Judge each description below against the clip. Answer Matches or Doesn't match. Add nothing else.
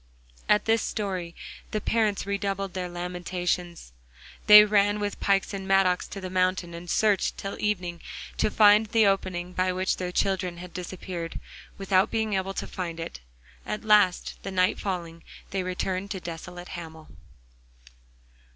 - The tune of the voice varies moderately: Doesn't match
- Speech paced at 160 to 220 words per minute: Doesn't match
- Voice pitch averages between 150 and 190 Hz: Matches